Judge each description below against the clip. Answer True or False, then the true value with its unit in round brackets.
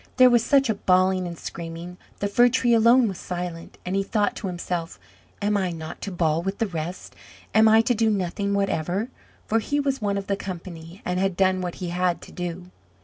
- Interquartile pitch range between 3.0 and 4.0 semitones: True (3.6 semitones)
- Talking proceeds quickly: True (215 wpm)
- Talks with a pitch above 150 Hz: True (190 Hz)